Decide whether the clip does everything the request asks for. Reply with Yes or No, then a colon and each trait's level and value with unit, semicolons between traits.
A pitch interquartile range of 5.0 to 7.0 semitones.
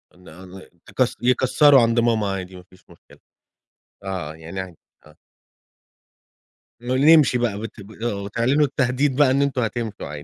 Yes: wide, 5.4 semitones